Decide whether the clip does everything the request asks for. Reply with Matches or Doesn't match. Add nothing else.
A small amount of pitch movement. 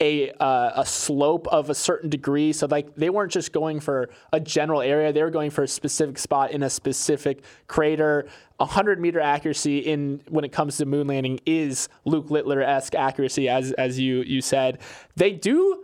Matches